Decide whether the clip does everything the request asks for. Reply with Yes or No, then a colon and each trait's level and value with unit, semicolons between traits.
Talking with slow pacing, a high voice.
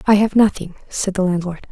No: fast, 210 wpm; high, 195 Hz